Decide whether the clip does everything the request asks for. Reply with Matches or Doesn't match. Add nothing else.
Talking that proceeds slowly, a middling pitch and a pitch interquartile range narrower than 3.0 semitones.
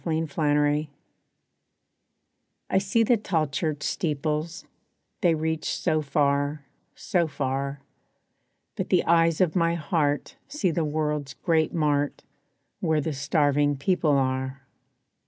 Matches